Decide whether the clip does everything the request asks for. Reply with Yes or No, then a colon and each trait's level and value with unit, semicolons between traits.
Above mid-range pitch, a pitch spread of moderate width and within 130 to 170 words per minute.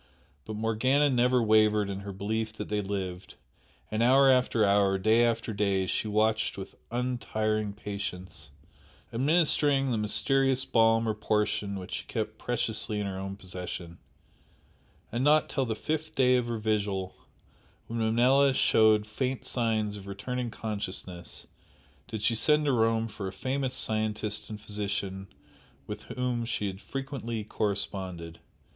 No: low, 110 Hz; average, 3.5 semitones; average, 145 wpm